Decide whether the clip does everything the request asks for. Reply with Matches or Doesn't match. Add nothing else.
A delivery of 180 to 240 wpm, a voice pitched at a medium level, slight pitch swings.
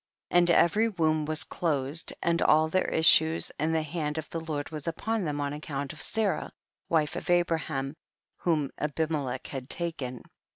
Doesn't match